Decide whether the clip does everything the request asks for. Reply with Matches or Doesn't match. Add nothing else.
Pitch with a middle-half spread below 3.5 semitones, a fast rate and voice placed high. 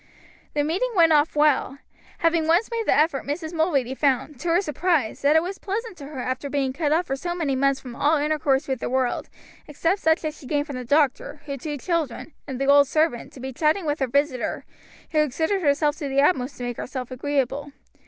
Matches